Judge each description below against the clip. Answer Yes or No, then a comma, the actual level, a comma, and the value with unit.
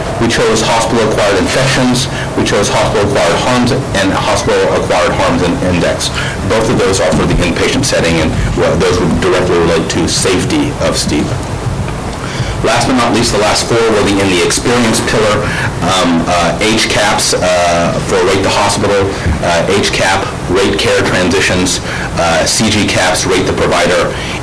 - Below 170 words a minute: Yes, average, 155 wpm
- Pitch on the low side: Yes, low, 105 Hz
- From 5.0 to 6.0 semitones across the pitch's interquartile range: Yes, wide, 5.5 semitones